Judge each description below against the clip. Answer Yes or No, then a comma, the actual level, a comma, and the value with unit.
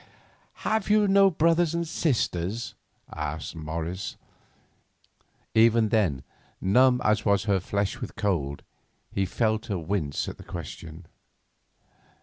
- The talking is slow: Yes, slow, 120 wpm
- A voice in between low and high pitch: No, low, 100 Hz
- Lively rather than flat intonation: Yes, wide, 6.8 semitones